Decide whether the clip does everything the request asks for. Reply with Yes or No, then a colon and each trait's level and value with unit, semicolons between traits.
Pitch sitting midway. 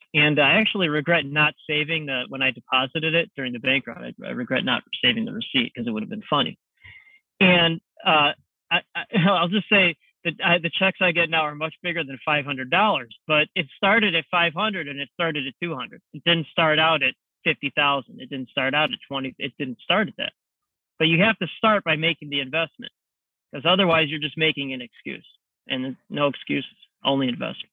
Yes: medium, 160 Hz